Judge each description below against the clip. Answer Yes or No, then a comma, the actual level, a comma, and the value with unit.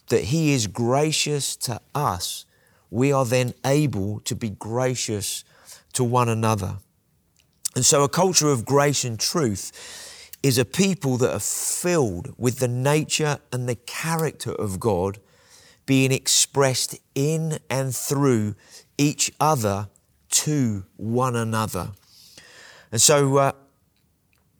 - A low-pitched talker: Yes, low, 130 Hz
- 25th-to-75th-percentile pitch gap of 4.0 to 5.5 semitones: Yes, average, 4.5 semitones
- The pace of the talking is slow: Yes, slow, 125 wpm